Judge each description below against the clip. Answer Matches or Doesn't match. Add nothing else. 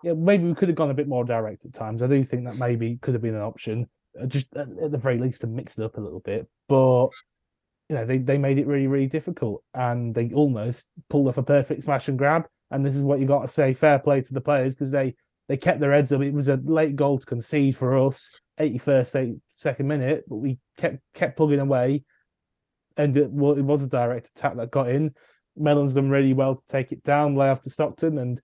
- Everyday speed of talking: Doesn't match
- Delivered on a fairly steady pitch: Matches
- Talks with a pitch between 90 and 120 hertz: Doesn't match